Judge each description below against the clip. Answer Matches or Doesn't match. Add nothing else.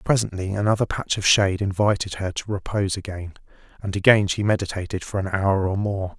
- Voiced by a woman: Doesn't match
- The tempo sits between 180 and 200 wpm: Matches